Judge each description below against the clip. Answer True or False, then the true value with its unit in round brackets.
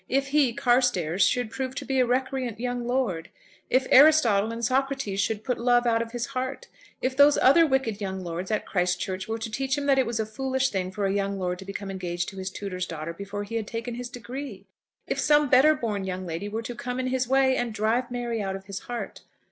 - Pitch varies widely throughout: False (4.8 semitones)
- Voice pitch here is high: True (235 Hz)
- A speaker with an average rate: False (235 wpm)